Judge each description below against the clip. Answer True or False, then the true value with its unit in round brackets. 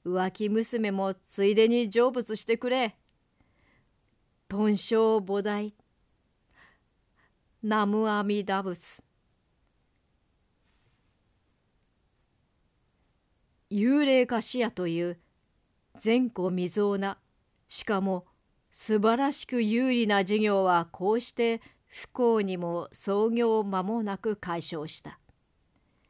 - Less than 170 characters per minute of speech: True (160 characters per minute)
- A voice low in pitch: False (205 Hz)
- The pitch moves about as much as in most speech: True (4.3 semitones)